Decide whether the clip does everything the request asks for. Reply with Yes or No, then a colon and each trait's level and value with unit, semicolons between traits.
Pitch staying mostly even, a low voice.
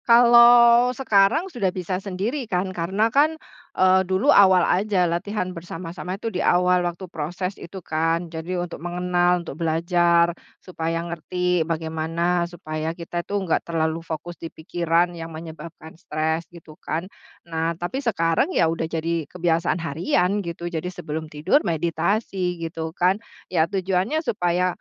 No: narrow, 2.2 semitones; medium, 175 Hz